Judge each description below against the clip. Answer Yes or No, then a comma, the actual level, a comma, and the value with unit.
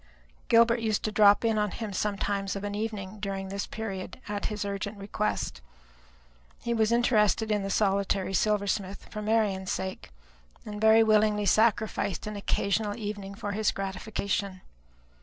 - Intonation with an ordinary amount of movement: No, narrow, 1.6 semitones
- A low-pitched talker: No, high, 205 Hz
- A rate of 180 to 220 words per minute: No, average, 150 wpm